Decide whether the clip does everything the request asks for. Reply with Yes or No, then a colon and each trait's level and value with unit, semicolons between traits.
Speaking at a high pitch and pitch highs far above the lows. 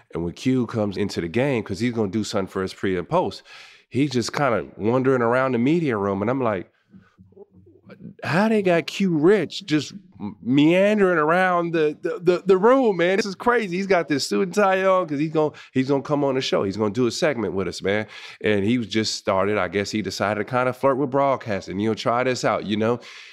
No: low, 130 Hz; wide, 7.9 semitones